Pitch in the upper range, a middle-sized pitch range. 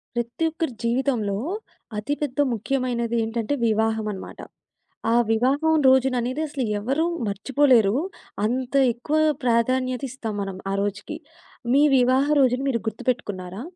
Yes: high, 245 Hz; average, 3.2 semitones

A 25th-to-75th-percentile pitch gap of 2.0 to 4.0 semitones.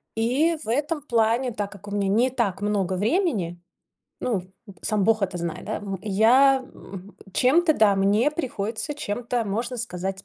No: average, 4.4 semitones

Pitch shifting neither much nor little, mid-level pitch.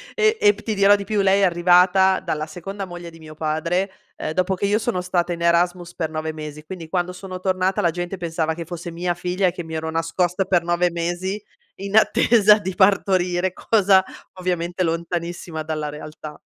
No: narrow, 2.3 semitones; medium, 175 Hz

